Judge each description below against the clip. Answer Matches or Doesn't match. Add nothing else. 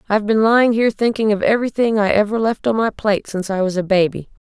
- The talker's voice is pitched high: Matches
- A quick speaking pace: Matches